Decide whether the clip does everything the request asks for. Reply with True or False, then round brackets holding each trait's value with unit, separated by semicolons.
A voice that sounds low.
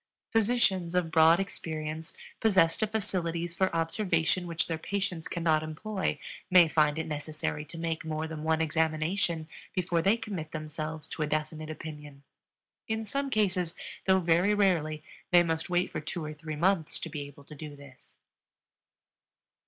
False (165 Hz)